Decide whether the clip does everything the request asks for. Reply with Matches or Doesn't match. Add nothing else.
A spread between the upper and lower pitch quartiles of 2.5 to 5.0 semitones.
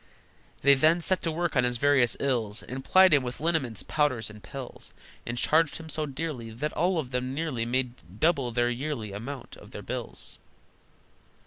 Matches